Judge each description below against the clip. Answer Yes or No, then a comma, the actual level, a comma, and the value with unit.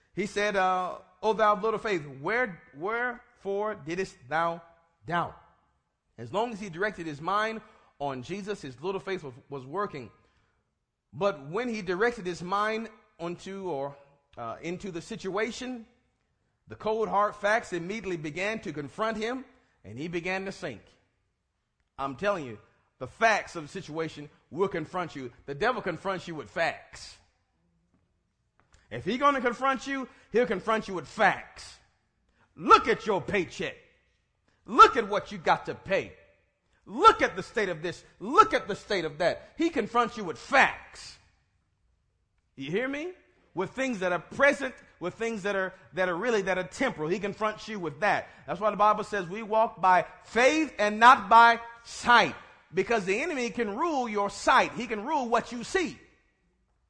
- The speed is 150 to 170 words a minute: Yes, average, 165 wpm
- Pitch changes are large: Yes, wide, 5.9 semitones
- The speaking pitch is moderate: No, high, 195 Hz